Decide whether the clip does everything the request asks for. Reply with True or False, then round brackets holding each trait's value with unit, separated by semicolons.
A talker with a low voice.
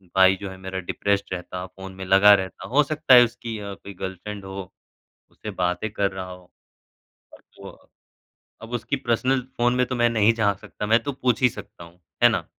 True (100 Hz)